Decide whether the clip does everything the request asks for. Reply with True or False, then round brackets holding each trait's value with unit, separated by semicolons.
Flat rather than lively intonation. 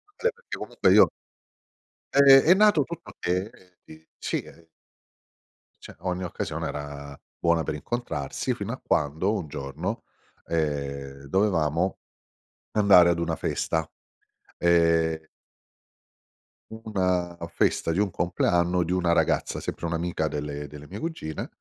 False (3.5 semitones)